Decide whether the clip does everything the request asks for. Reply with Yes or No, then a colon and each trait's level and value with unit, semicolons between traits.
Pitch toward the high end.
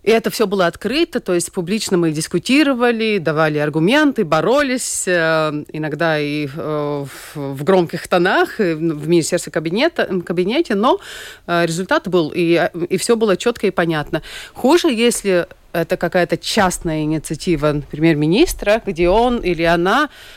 No: medium, 175 Hz